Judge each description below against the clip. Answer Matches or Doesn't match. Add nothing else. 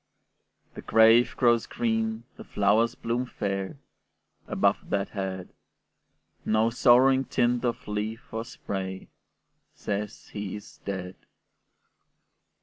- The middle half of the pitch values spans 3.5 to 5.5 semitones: Doesn't match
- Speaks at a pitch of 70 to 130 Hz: Matches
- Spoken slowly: Matches